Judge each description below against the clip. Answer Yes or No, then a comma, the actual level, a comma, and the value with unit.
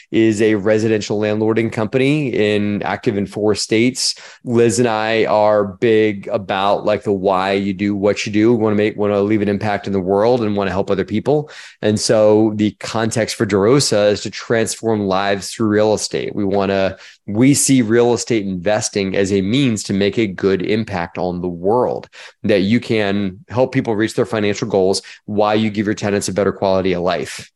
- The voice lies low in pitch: Yes, low, 105 Hz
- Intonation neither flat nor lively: No, narrow, 2.0 semitones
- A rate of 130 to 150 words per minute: No, fast, 205 wpm